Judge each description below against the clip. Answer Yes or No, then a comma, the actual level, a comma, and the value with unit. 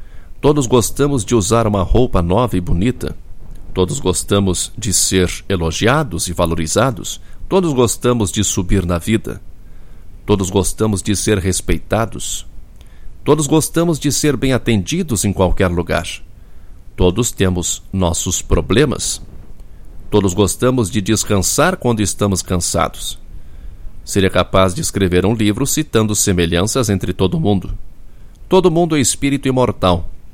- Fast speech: No, average, 125 wpm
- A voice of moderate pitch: No, low, 100 Hz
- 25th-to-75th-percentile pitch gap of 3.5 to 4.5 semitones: No, average, 4.9 semitones